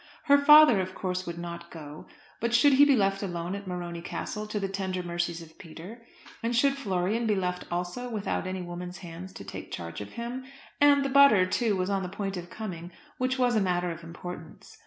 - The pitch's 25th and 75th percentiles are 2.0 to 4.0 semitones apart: No, average, 5.0 semitones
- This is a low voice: No, high, 190 Hz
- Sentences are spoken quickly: Yes, fast, 215 wpm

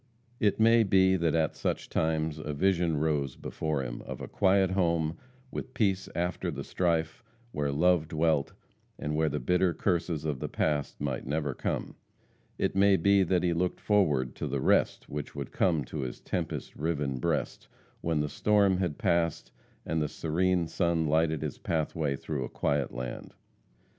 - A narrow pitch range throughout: No, average, 3.6 semitones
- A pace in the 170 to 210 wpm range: Yes, average, 175 wpm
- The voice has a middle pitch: No, very low, 80 Hz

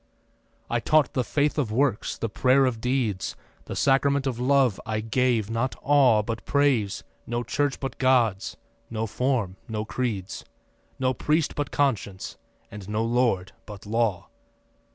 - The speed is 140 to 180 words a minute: Yes, average, 150 wpm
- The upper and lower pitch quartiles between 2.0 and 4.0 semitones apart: Yes, average, 3.7 semitones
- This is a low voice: Yes, low, 120 Hz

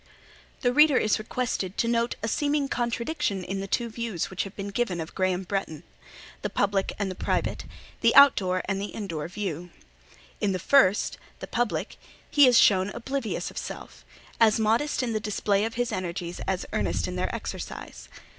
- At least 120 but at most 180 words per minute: Yes, average, 175 wpm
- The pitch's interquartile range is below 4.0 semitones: No, average, 4.3 semitones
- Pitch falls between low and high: No, high, 210 Hz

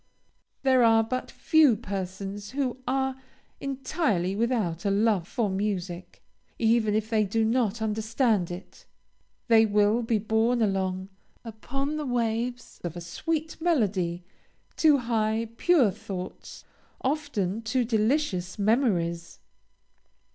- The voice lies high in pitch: Yes, high, 220 Hz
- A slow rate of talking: Yes, slow, 120 wpm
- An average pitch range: Yes, average, 4.2 semitones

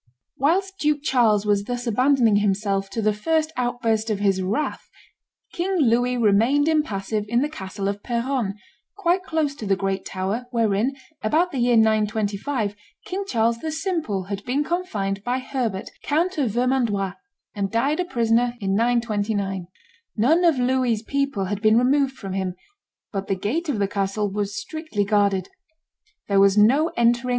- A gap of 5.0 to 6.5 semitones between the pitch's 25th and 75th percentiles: Yes, average, 5.3 semitones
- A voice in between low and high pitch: No, high, 230 Hz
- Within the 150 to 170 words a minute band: Yes, average, 160 wpm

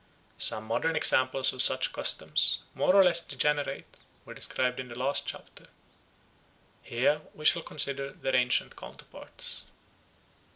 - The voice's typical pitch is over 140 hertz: No, low, 135 Hz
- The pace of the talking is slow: Yes, slow, 130 wpm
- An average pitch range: Yes, average, 3.1 semitones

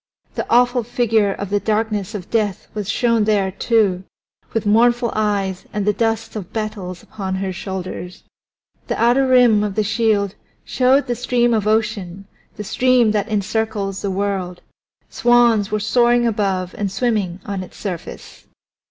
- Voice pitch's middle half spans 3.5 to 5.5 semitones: No, average, 2.9 semitones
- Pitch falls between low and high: No, high, 210 Hz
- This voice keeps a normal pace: Yes, average, 155 wpm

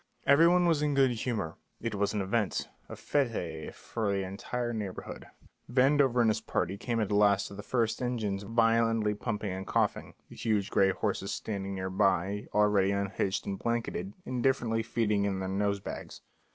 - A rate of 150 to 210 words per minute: Yes, average, 170 wpm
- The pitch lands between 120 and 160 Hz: No, low, 105 Hz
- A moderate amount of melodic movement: Yes, average, 3.2 semitones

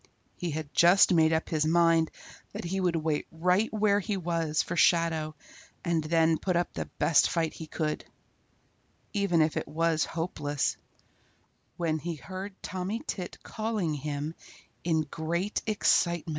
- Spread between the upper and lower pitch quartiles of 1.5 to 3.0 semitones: Yes, narrow, 2.4 semitones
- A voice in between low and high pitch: Yes, medium, 165 Hz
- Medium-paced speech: Yes, average, 155 wpm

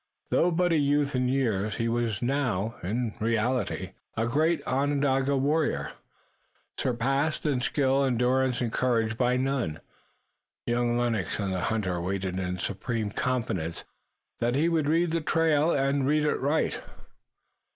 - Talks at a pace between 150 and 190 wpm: No, average, 140 wpm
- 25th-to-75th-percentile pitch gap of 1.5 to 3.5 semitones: No, average, 4.3 semitones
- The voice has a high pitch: No, low, 125 Hz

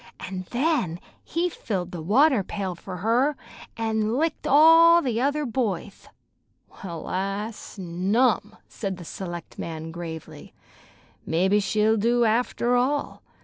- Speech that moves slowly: Yes, slow, 120 wpm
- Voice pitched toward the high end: Yes, high, 215 Hz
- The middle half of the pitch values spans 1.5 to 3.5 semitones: No, wide, 5.5 semitones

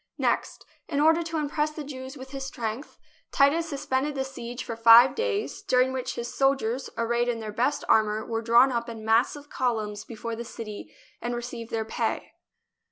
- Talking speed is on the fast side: No, average, 185 wpm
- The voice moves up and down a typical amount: Yes, average, 3.3 semitones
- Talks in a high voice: Yes, high, 245 Hz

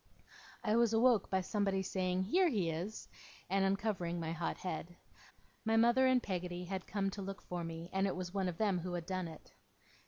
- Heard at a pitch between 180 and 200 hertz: Yes, high, 190 Hz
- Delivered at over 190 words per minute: Yes, fast, 205 wpm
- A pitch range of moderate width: Yes, average, 3.0 semitones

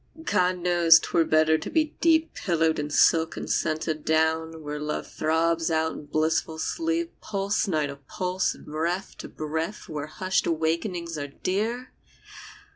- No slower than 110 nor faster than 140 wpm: No, average, 155 wpm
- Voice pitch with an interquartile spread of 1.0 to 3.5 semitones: Yes, average, 2.8 semitones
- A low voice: No, medium, 165 Hz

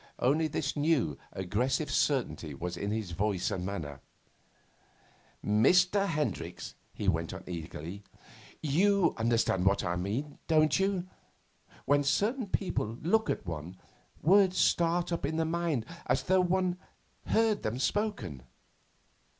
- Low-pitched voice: No, medium, 145 Hz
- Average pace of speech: No, slow, 130 wpm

